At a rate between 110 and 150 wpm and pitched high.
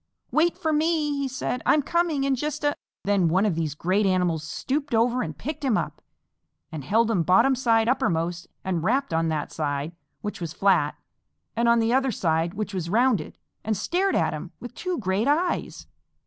No: average, 195 wpm; high, 220 Hz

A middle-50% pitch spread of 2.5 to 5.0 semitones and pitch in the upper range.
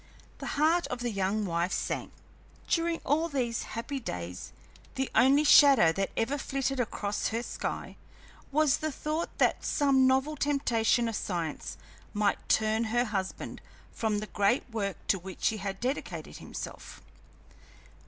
No: wide, 5.6 semitones; high, 235 Hz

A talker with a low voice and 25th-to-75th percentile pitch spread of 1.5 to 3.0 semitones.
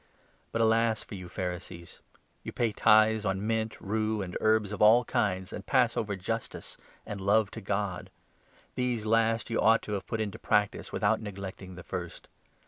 Yes: low, 105 Hz; narrow, 2.5 semitones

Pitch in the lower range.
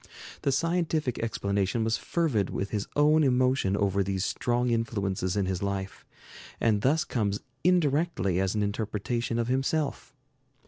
Yes: low, 115 Hz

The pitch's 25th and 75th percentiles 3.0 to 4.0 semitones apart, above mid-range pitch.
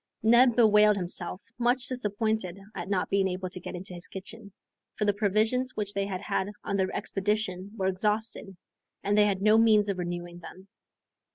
No: narrow, 2.6 semitones; high, 200 Hz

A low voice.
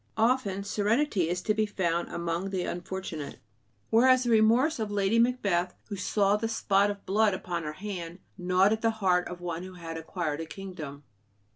No: high, 195 Hz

